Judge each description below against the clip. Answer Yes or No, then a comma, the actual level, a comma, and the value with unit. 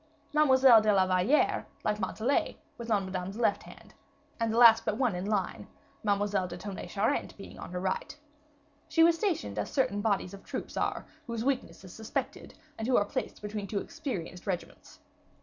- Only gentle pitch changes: No, average, 3.7 semitones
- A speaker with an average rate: Yes, average, 185 wpm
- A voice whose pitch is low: No, high, 210 Hz